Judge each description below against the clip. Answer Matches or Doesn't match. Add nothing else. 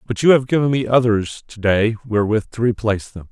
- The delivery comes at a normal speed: Doesn't match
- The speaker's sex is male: Matches